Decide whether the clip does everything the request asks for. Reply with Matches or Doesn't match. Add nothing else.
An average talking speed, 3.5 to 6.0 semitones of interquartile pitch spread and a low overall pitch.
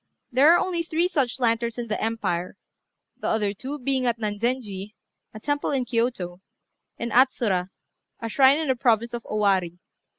Doesn't match